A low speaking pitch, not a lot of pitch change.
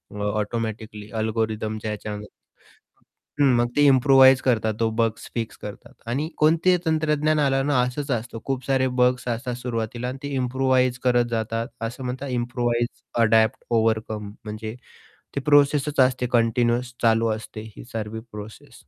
No: low, 120 Hz; average, 3.0 semitones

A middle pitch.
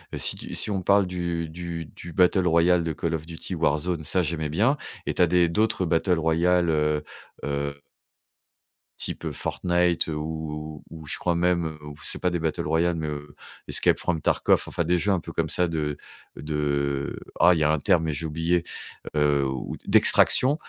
No: very low, 80 Hz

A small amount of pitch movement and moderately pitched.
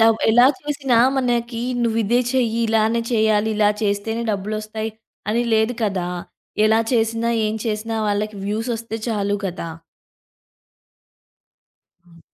No: narrow, 1.6 semitones; high, 220 Hz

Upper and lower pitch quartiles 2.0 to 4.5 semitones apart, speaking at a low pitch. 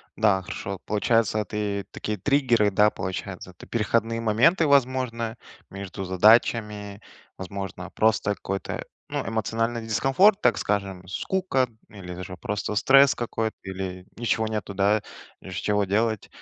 Yes: average, 2.9 semitones; low, 105 Hz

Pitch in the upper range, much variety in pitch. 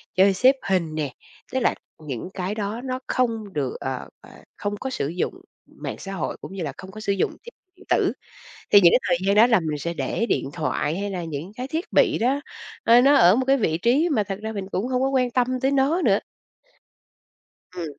Yes: high, 205 Hz; wide, 6.5 semitones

